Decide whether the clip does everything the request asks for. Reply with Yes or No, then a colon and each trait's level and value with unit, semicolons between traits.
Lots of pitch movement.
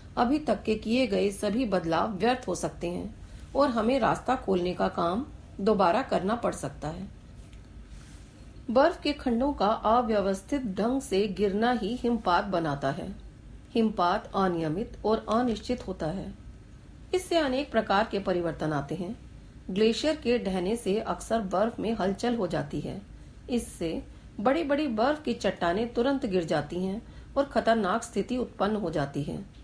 No: average, 4.7 semitones